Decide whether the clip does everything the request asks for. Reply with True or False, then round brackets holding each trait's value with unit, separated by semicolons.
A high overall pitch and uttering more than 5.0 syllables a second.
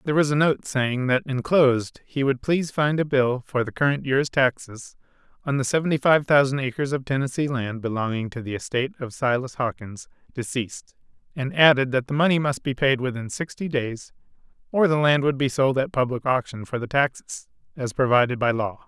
False (135 Hz; 5.5 syllables/s)